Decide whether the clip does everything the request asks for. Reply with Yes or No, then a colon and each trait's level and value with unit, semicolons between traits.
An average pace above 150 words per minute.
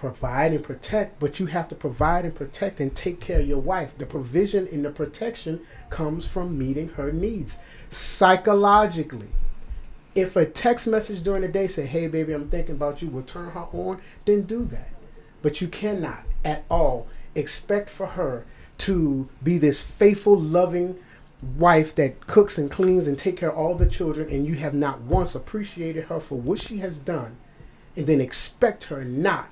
Yes: average, 185 wpm